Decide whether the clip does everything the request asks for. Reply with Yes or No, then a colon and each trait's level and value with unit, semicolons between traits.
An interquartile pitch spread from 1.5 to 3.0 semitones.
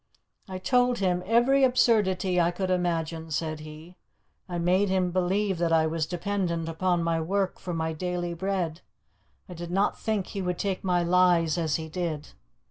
Yes: narrow, 2.5 semitones